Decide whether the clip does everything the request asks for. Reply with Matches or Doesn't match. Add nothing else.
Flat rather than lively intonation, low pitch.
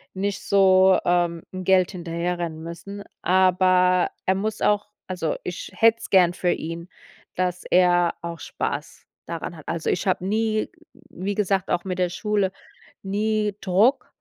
Doesn't match